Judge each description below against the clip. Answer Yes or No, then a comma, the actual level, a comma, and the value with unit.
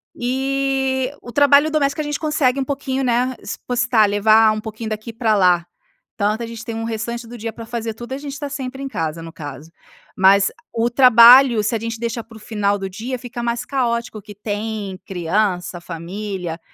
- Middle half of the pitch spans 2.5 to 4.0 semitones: Yes, average, 3.7 semitones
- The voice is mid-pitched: No, high, 230 Hz